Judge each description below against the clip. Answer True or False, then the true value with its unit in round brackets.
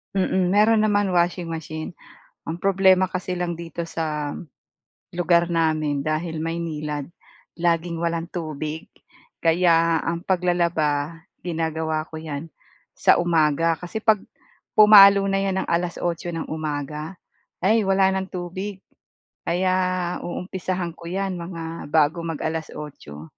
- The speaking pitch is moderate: True (170 Hz)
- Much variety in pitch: False (2.5 semitones)